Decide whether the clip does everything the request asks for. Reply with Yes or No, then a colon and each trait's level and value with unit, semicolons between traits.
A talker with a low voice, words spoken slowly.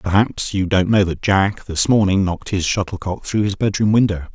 No: very low, 95 Hz; fast, 205 wpm